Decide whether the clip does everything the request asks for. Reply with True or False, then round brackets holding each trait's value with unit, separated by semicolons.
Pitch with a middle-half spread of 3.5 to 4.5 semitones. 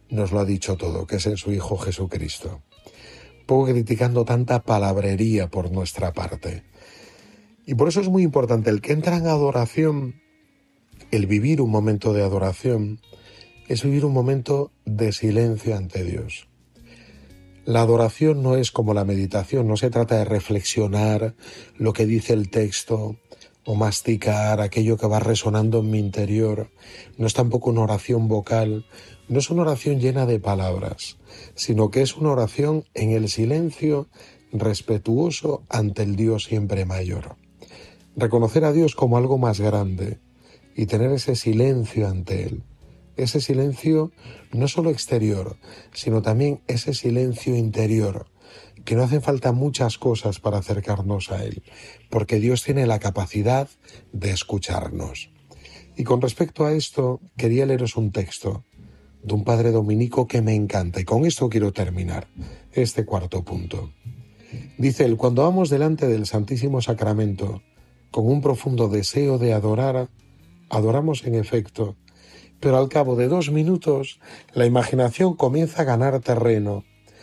True (3.8 semitones)